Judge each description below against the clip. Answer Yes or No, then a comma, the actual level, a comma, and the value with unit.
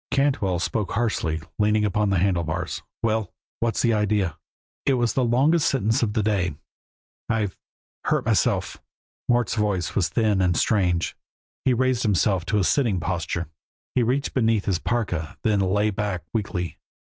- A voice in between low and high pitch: No, low, 105 Hz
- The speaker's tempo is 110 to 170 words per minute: Yes, average, 160 wpm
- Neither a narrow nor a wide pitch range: Yes, average, 3.8 semitones